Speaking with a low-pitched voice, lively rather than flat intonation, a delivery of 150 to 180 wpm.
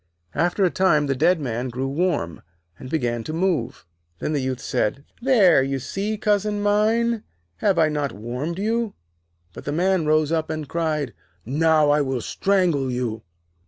No: medium, 155 Hz; wide, 6.0 semitones; average, 165 wpm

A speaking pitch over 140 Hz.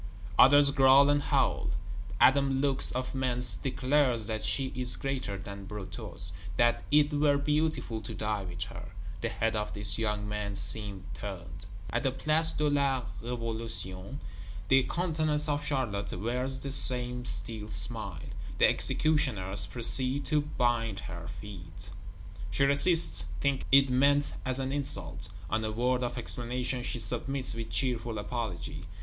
No: low, 125 Hz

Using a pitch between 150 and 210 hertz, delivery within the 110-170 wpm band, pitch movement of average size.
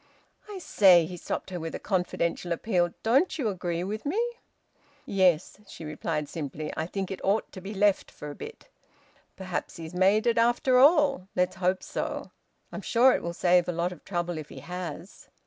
No: medium, 185 Hz; average, 190 wpm; average, 4.0 semitones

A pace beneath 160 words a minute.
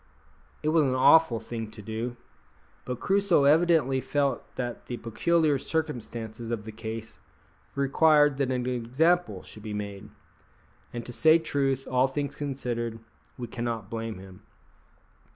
Yes: average, 140 wpm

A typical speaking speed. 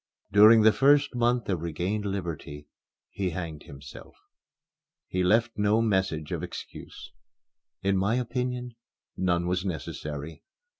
No: slow, 120 wpm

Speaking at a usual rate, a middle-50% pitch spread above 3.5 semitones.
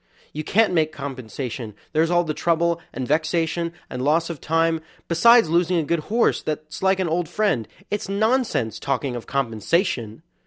Yes: average, 165 wpm; average, 3.9 semitones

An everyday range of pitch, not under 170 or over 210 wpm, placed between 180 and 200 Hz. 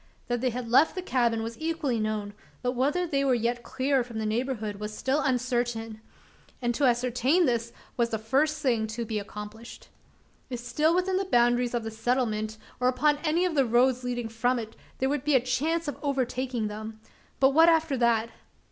No: average, 3.4 semitones; average, 200 wpm; high, 245 Hz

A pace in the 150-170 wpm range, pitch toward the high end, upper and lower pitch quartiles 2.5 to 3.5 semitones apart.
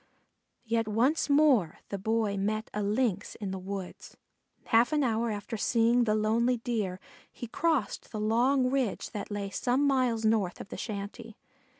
Yes: average, 165 wpm; high, 225 Hz; average, 3.0 semitones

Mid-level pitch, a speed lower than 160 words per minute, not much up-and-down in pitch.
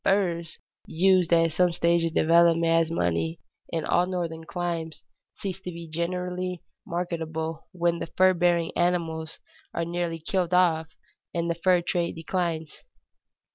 Yes: medium, 170 Hz; average, 140 wpm; narrow, 1.5 semitones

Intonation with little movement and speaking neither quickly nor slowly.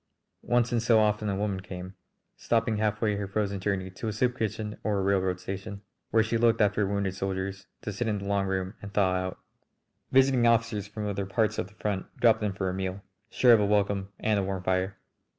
No: narrow, 2.2 semitones; fast, 220 wpm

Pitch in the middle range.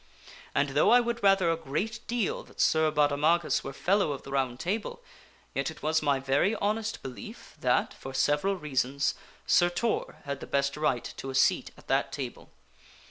Yes: medium, 150 Hz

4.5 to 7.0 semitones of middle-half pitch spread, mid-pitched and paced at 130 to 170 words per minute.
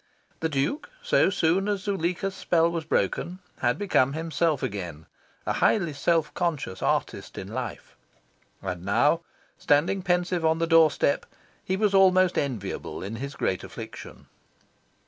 Yes: average, 4.8 semitones; medium, 165 Hz; average, 140 wpm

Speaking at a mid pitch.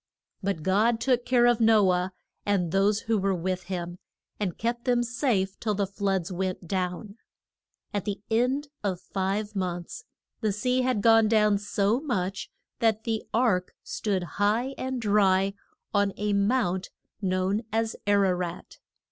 No: high, 205 Hz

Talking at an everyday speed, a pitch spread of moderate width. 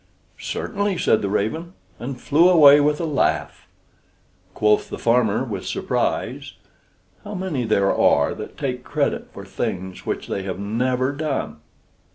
No: average, 145 wpm; wide, 6.3 semitones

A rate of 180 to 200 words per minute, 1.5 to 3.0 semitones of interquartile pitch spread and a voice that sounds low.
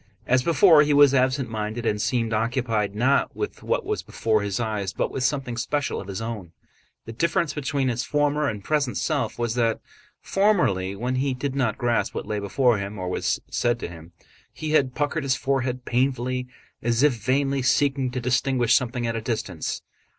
No: average, 190 wpm; average, 3.7 semitones; low, 125 Hz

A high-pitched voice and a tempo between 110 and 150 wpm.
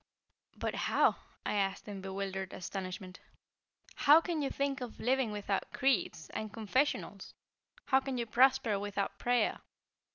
Yes: high, 220 Hz; slow, 135 wpm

